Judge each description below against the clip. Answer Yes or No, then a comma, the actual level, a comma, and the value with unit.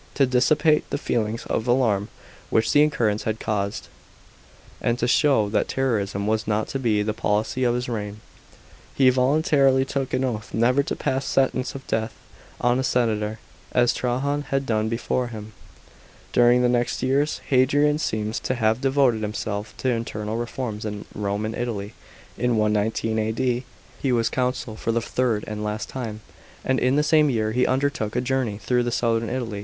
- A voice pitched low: Yes, low, 120 Hz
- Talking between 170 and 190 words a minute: Yes, average, 175 wpm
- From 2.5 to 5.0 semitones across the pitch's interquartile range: Yes, average, 3.2 semitones